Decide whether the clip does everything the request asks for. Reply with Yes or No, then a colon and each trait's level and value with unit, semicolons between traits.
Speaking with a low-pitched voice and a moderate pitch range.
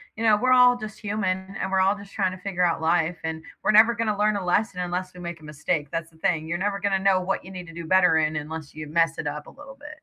No: medium, 185 Hz; average, 3.9 semitones